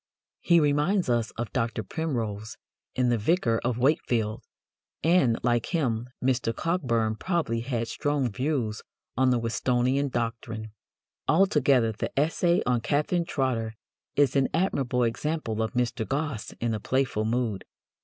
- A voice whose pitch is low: Yes, low, 125 Hz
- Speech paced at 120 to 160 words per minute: Yes, slow, 135 wpm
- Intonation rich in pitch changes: No, average, 4.2 semitones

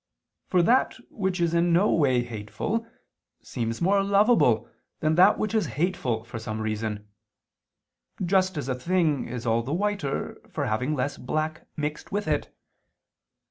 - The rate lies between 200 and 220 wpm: No, average, 150 wpm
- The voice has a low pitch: No, medium, 155 Hz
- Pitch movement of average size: No, wide, 7.6 semitones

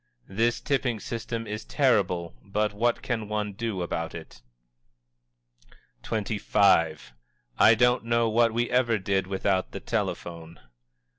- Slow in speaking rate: Yes, slow, 125 wpm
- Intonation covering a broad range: No, average, 3.6 semitones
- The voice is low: Yes, low, 105 Hz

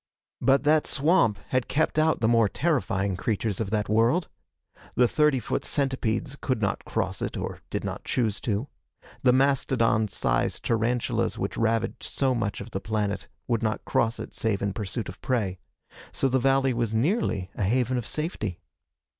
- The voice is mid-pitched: No, low, 115 Hz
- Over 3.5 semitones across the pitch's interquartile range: Yes, average, 4.0 semitones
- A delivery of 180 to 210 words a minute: No, average, 170 wpm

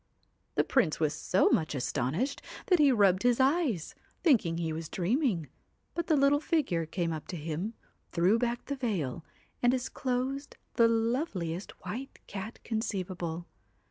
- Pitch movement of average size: No, wide, 7.7 semitones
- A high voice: Yes, high, 220 Hz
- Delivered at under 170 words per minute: Yes, average, 145 wpm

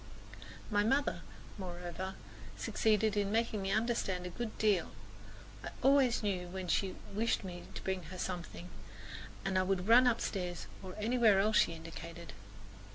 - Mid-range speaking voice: No, high, 195 Hz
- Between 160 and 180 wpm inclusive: No, average, 150 wpm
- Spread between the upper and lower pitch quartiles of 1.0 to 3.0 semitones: No, average, 3.4 semitones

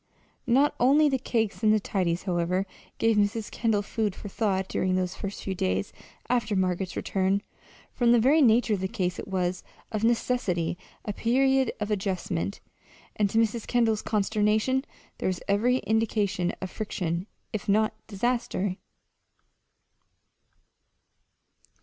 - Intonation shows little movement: No, average, 3.6 semitones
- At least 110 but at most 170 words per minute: Yes, average, 140 wpm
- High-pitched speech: Yes, high, 210 Hz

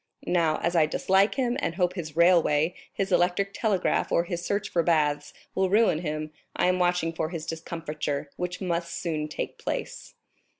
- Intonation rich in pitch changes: No, average, 2.7 semitones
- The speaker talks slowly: No, average, 175 wpm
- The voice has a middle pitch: Yes, medium, 170 Hz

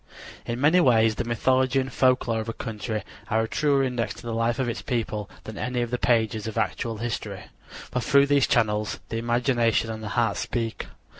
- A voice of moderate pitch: No, low, 120 Hz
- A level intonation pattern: Yes, narrow, 2.3 semitones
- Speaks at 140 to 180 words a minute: No, fast, 205 wpm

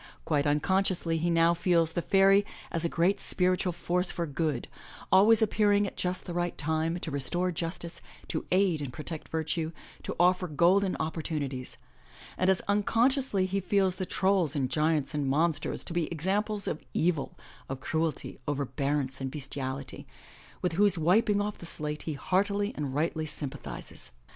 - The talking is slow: No, average, 160 wpm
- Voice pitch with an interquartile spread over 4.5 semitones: No, average, 3.9 semitones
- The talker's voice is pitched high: No, medium, 170 Hz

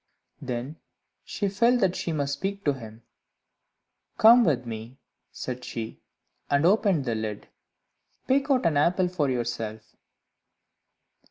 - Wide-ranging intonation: Yes, wide, 8.4 semitones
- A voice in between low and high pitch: Yes, medium, 145 Hz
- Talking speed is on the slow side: Yes, slow, 125 wpm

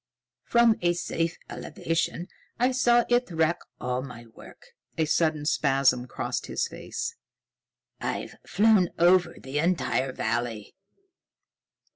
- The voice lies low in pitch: No, medium, 165 Hz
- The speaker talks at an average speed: No, slow, 115 wpm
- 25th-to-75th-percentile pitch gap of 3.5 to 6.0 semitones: Yes, wide, 5.5 semitones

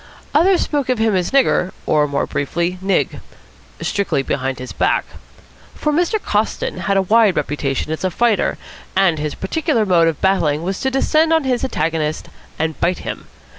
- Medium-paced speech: Yes, average, 170 wpm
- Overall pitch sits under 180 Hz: No, high, 190 Hz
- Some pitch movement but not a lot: No, wide, 8.0 semitones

